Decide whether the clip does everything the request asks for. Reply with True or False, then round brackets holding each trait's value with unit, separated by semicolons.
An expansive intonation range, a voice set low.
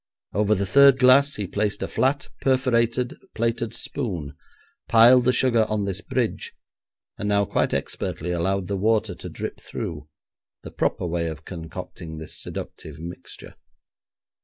True (5.7 semitones; 105 Hz)